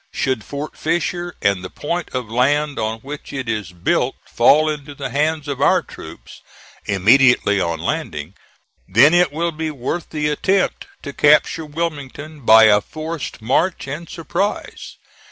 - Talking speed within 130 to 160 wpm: Yes, average, 155 wpm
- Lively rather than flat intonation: Yes, wide, 5.7 semitones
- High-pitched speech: No, medium, 145 Hz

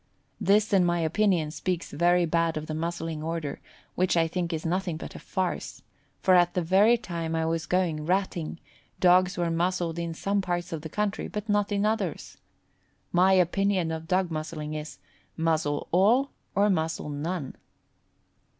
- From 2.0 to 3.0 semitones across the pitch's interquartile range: Yes, average, 2.7 semitones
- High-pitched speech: No, medium, 175 Hz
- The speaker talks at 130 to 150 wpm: No, average, 170 wpm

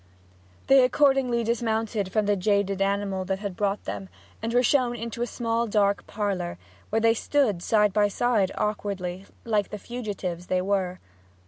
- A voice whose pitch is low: No, high, 210 Hz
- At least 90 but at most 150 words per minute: No, average, 160 wpm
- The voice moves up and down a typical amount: Yes, average, 3.1 semitones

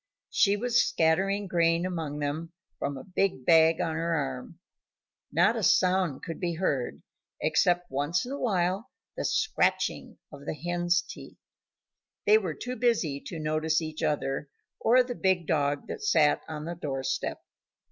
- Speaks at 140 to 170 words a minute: Yes, average, 160 wpm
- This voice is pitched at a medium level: Yes, medium, 165 Hz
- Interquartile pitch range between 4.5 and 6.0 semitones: No, average, 4.0 semitones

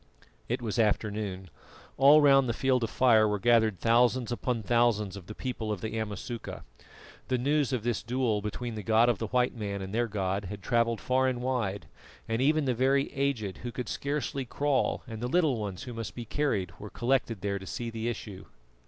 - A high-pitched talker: No, low, 115 Hz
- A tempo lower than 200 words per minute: No, fast, 205 wpm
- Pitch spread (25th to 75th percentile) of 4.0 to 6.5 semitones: No, average, 3.4 semitones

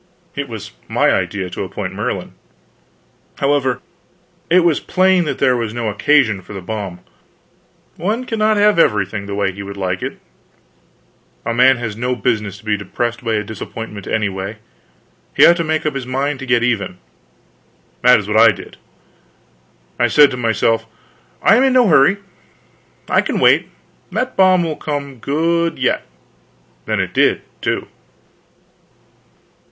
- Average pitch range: No, wide, 6.7 semitones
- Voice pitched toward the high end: No, low, 125 Hz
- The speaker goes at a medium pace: Yes, average, 160 wpm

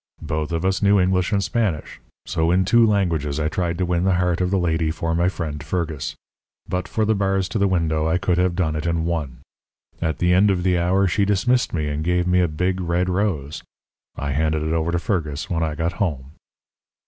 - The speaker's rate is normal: No, fast, 225 wpm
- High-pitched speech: No, very low, 85 Hz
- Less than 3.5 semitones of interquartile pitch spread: Yes, average, 2.8 semitones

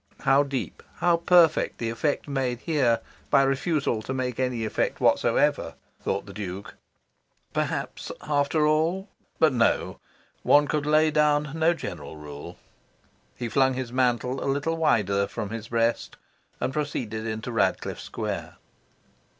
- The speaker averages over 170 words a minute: No, average, 140 wpm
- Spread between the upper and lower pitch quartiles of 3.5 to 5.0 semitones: Yes, average, 4.6 semitones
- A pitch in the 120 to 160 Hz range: Yes, low, 135 Hz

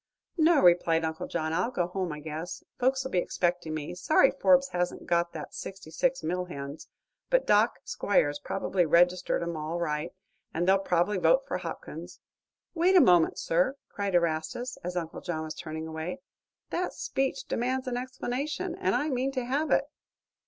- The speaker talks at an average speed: Yes, average, 175 wpm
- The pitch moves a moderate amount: No, wide, 7.9 semitones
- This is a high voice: No, medium, 180 Hz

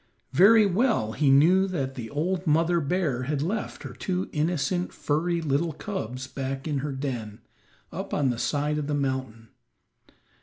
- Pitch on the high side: No, medium, 150 Hz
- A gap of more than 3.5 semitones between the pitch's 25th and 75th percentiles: Yes, average, 4.8 semitones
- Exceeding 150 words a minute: Yes, average, 160 wpm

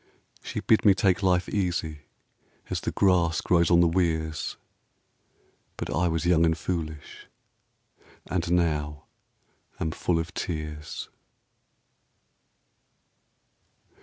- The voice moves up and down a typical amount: No, narrow, 2.1 semitones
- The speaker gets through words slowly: Yes, slow, 105 wpm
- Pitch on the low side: Yes, very low, 85 Hz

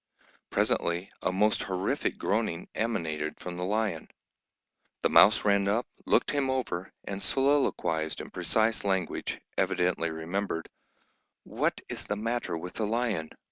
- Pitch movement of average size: Yes, average, 4.6 semitones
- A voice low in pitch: Yes, low, 100 Hz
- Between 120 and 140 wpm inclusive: Yes, slow, 135 wpm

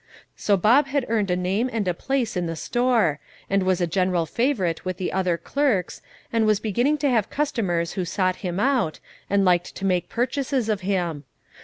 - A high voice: Yes, high, 195 Hz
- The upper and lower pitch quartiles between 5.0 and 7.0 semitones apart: Yes, average, 5.3 semitones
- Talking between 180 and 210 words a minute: Yes, average, 195 wpm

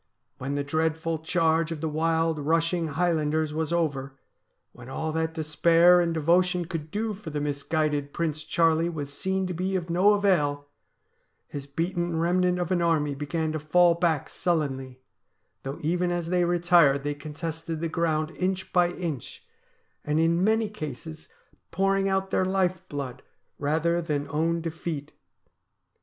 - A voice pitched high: No, medium, 165 Hz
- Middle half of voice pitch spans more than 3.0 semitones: No, average, 2.7 semitones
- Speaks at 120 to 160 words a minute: Yes, average, 155 wpm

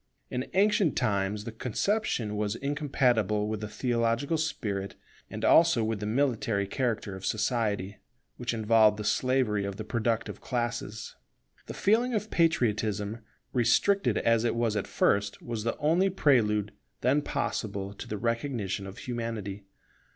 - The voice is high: No, low, 115 Hz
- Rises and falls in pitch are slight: No, average, 3.7 semitones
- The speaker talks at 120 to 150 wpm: Yes, average, 145 wpm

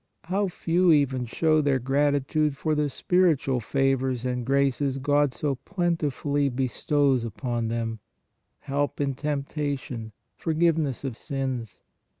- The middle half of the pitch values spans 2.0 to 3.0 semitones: Yes, average, 2.7 semitones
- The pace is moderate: No, slow, 120 wpm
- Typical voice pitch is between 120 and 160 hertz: Yes, medium, 140 Hz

